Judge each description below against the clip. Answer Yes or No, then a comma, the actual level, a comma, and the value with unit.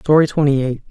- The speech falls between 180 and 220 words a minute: Yes, average, 200 wpm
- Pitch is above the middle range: No, medium, 145 Hz